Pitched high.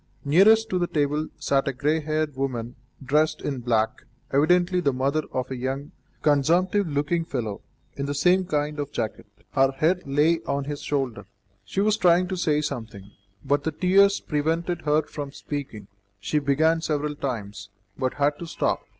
No: medium, 145 Hz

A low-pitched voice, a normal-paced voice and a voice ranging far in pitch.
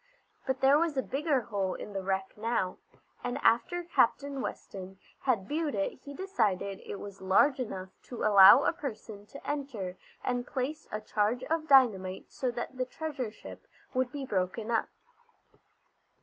No: high, 245 Hz; average, 165 wpm; wide, 5.8 semitones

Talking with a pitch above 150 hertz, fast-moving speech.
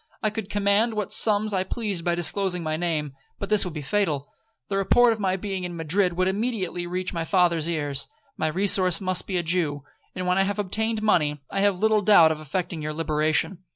Yes: medium, 185 Hz; fast, 215 wpm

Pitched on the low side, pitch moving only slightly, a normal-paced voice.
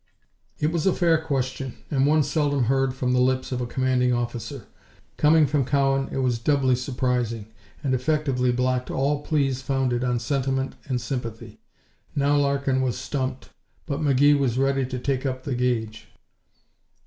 Yes: low, 130 Hz; narrow, 2.0 semitones; average, 160 wpm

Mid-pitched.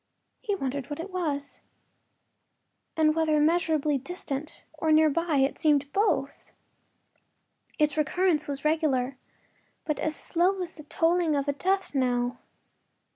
No: very high, 305 Hz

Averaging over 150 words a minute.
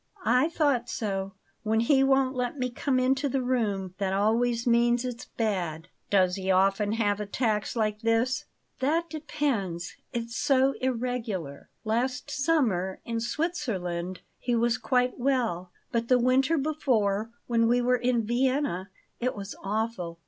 No: average, 145 wpm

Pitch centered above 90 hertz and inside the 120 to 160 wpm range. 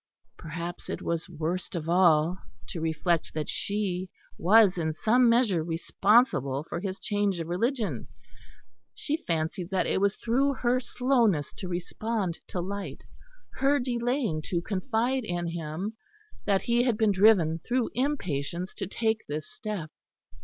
Yes: high, 190 Hz; average, 145 wpm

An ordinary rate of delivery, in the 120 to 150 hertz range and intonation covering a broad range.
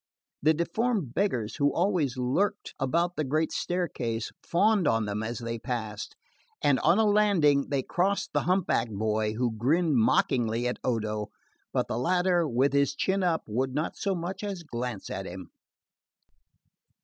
Yes: average, 160 wpm; medium, 140 Hz; wide, 7.3 semitones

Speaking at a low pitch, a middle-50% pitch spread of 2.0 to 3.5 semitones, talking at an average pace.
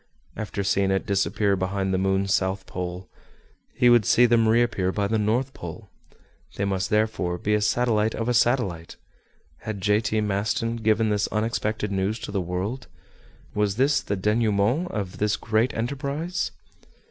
Yes: low, 105 Hz; average, 2.9 semitones; average, 160 wpm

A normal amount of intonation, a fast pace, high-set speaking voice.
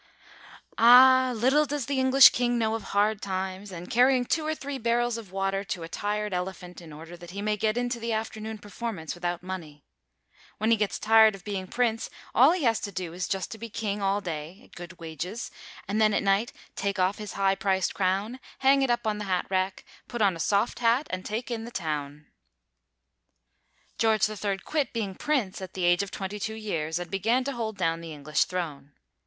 Yes: average, 4.0 semitones; fast, 210 wpm; high, 205 Hz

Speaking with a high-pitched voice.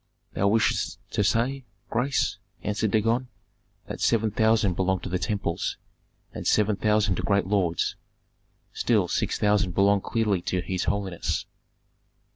No: low, 105 Hz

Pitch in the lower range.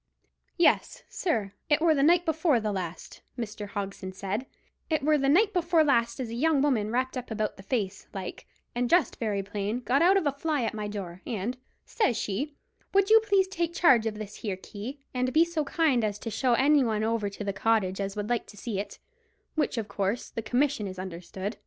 No: high, 235 Hz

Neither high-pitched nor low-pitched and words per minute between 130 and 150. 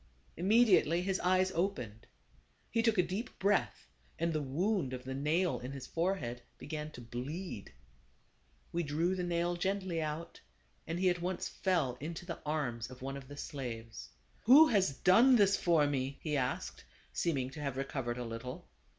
No: medium, 160 Hz; average, 175 wpm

